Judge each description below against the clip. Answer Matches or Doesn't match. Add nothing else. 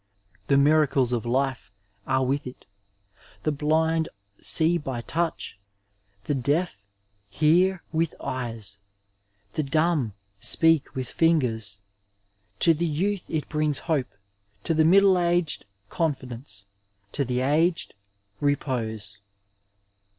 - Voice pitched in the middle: Matches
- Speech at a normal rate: Doesn't match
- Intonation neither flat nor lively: Matches